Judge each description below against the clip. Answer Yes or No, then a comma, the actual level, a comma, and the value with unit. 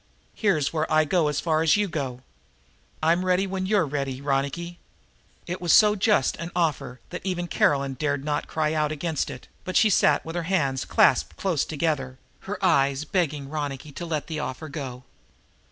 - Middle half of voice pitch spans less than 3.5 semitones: No, average, 3.9 semitones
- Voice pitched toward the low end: No, medium, 155 Hz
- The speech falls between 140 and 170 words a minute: No, average, 185 wpm